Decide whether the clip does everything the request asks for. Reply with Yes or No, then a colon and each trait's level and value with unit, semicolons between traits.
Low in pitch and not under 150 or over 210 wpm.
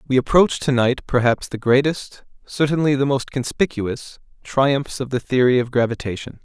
Yes: low, 130 Hz; average, 160 wpm